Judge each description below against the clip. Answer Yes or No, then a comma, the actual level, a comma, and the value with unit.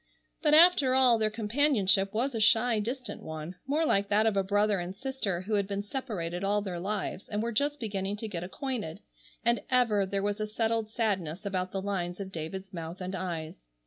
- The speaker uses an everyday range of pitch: Yes, average, 3.6 semitones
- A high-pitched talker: Yes, high, 205 Hz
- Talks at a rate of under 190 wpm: No, fast, 205 wpm